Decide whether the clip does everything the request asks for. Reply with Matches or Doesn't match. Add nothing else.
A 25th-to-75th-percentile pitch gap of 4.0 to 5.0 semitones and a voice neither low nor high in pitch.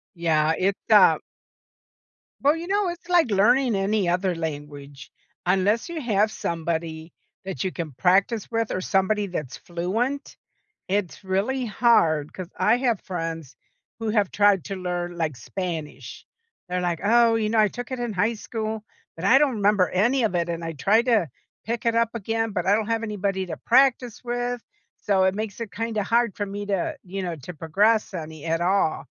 Doesn't match